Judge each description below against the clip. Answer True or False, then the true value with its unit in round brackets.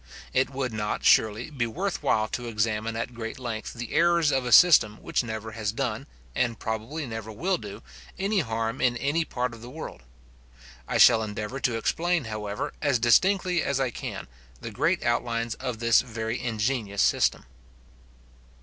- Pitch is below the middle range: True (120 Hz)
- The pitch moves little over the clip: False (3.6 semitones)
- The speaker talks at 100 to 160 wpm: False (170 wpm)